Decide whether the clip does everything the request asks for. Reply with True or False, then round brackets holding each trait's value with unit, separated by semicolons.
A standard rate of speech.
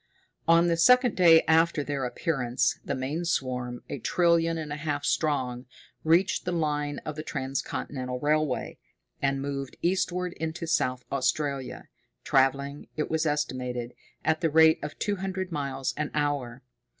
True (150 wpm)